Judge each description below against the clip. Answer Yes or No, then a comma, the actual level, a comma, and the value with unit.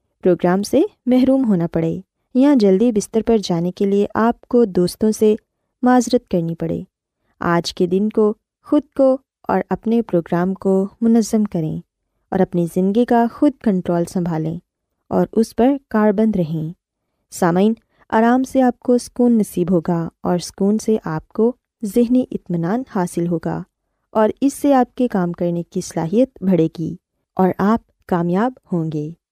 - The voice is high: Yes, high, 205 Hz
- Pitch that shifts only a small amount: No, average, 5.1 semitones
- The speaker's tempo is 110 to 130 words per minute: No, average, 155 wpm